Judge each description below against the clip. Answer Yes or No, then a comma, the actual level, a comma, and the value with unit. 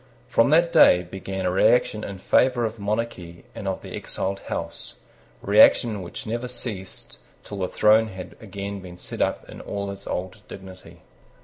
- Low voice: Yes, low, 100 Hz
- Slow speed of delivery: No, average, 170 wpm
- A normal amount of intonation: Yes, average, 3.1 semitones